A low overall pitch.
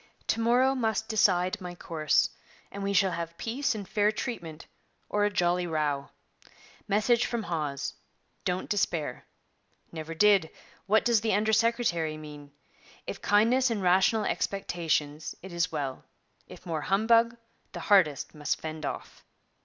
No: high, 190 Hz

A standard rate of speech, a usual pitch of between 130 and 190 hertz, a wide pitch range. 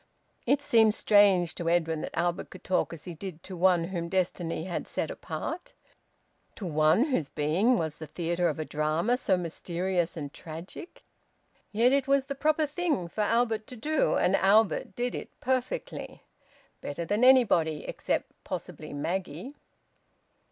Yes: average, 160 wpm; medium, 185 Hz; wide, 6.4 semitones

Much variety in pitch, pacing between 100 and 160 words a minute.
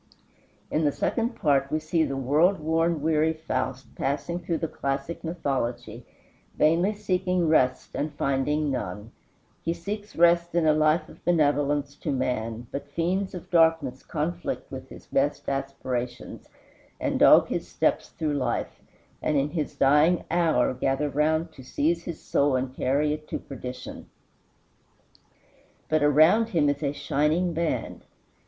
No: average, 3.4 semitones; average, 150 wpm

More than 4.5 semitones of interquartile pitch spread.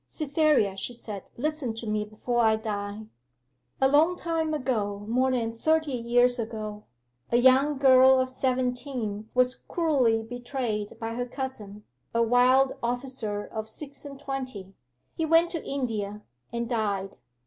No: average, 3.7 semitones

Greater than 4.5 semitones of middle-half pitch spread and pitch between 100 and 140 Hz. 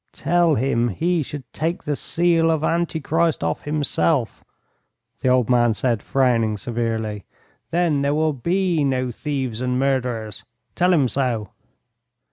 Yes: average, 5.2 semitones; low, 135 Hz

